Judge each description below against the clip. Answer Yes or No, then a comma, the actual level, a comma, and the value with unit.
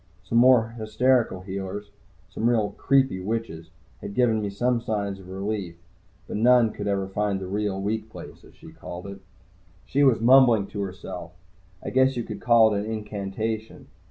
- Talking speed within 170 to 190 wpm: Yes, average, 175 wpm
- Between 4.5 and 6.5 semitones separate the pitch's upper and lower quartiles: No, average, 3.1 semitones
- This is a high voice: No, low, 105 Hz